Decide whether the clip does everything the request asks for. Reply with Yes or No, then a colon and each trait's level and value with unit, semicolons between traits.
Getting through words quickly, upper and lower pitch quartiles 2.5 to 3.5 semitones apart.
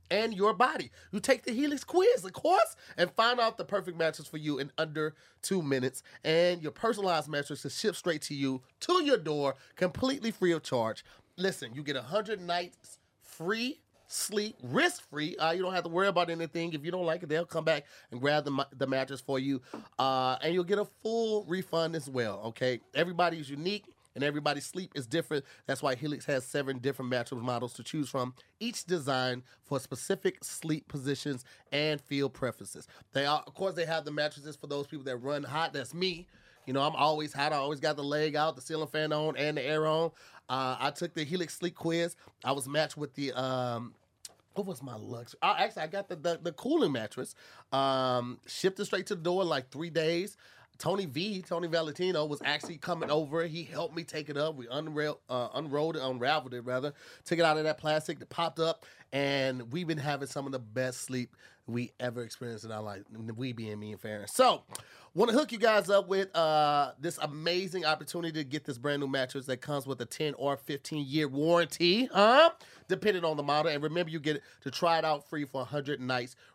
No: fast, 215 wpm; average, 4.3 semitones